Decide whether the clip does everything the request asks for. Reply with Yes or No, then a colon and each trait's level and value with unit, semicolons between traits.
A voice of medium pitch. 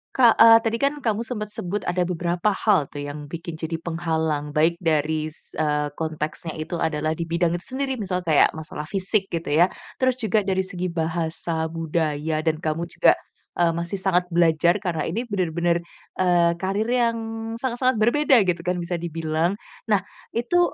Yes: medium, 170 Hz